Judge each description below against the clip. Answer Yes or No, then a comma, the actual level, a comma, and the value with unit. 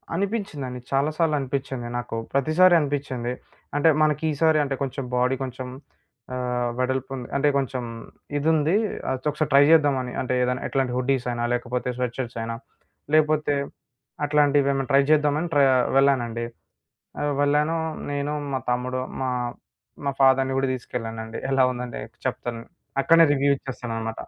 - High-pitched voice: No, low, 135 Hz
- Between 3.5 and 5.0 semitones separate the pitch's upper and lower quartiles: No, average, 2.8 semitones